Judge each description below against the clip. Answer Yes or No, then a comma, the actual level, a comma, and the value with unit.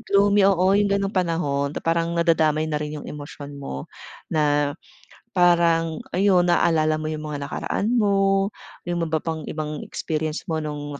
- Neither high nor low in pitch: Yes, medium, 160 Hz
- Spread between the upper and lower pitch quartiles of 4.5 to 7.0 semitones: No, average, 2.9 semitones